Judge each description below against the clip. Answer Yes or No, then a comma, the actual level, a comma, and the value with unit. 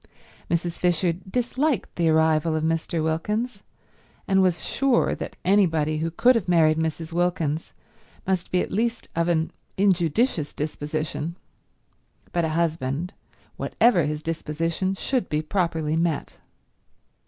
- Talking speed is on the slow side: Yes, slow, 130 wpm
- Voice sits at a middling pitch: Yes, medium, 165 Hz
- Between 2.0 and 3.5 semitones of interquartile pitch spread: Yes, average, 3.0 semitones